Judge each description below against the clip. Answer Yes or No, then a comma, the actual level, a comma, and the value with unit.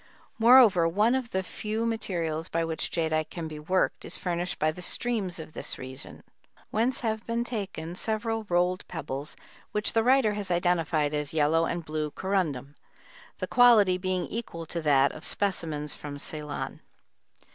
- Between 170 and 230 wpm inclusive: No, average, 160 wpm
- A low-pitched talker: No, medium, 175 Hz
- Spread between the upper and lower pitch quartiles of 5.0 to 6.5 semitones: Yes, wide, 5.4 semitones